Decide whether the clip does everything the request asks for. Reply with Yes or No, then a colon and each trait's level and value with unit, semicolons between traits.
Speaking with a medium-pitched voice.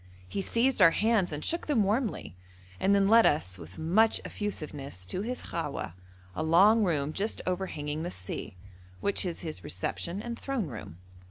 Yes: medium, 180 Hz